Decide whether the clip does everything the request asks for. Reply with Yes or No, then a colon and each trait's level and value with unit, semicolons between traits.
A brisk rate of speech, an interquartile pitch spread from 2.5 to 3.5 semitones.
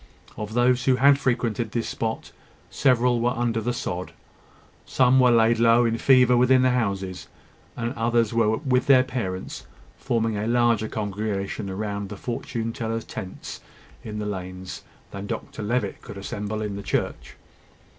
No: average, 155 wpm; average, 2.9 semitones